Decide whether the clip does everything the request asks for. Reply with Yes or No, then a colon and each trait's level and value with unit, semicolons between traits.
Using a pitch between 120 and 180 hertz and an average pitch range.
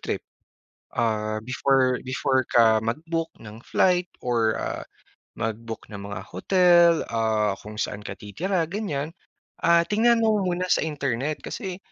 No: low, 135 Hz; wide, 7.8 semitones